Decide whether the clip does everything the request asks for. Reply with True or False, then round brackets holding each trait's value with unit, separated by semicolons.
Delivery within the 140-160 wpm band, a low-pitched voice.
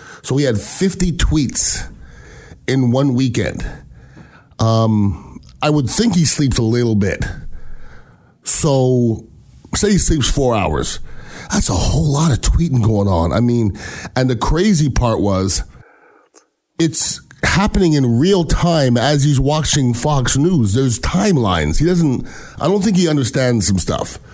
True (145 wpm; 130 Hz)